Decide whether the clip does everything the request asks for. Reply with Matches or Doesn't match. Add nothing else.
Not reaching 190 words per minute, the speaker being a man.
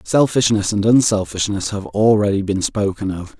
Matches